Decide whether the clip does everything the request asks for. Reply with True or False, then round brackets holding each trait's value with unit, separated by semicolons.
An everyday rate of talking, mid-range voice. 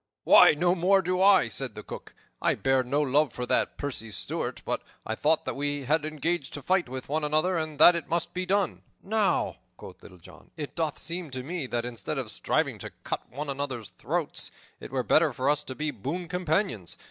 False (215 wpm; 150 Hz)